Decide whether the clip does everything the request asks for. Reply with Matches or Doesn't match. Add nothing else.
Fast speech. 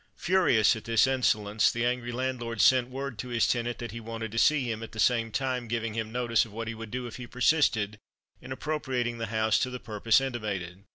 Matches